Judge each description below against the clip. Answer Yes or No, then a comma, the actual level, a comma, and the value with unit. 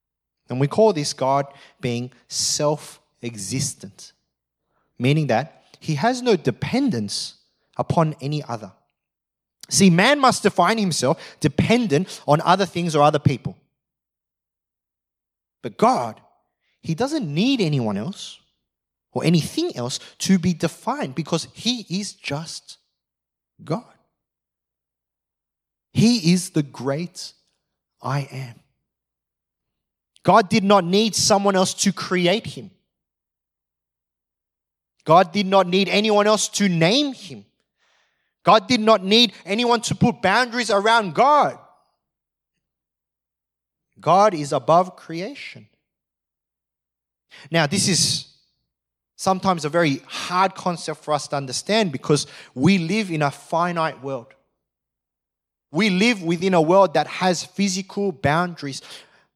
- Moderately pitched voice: Yes, medium, 165 Hz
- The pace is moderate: No, slow, 115 wpm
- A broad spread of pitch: Yes, wide, 6.7 semitones